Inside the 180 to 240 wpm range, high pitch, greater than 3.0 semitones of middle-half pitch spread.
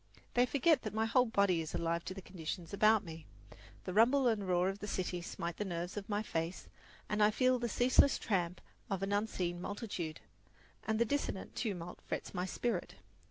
Yes: average, 195 wpm; high, 200 Hz; average, 4.0 semitones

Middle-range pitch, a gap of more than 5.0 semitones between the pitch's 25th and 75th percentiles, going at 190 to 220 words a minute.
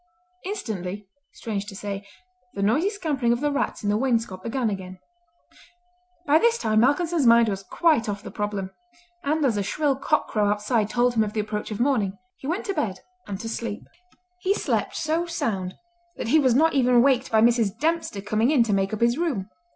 No: high, 230 Hz; wide, 5.6 semitones; average, 200 wpm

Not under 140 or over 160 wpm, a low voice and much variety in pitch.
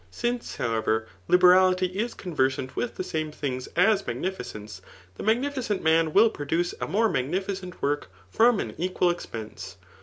No: average, 155 wpm; medium, 180 Hz; wide, 6.8 semitones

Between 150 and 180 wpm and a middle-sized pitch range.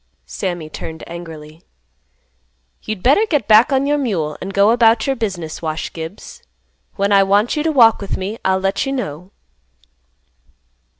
No: average, 160 wpm; wide, 6.1 semitones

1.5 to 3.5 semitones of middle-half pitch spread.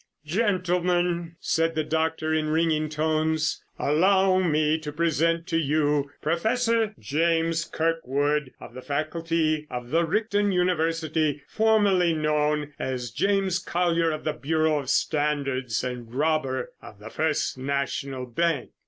Yes: narrow, 2.4 semitones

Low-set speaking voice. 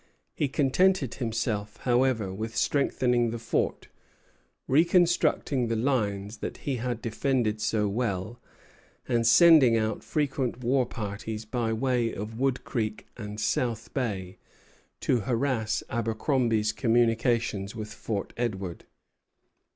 Yes: low, 115 Hz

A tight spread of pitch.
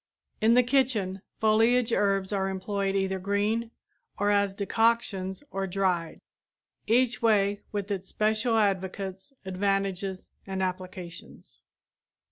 Yes: narrow, 2.3 semitones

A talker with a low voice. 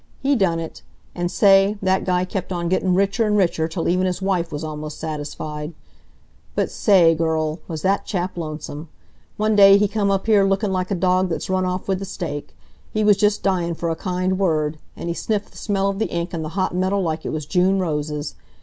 No: medium, 185 Hz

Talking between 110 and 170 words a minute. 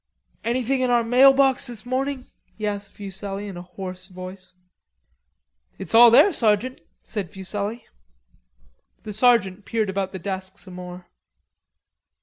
Yes: slow, 135 wpm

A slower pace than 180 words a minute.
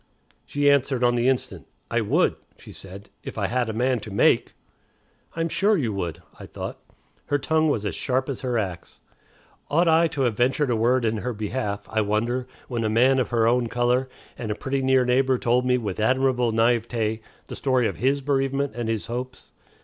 No: fast, 205 wpm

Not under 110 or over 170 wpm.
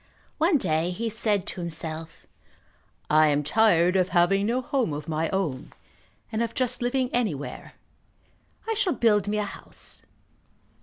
Yes: average, 150 wpm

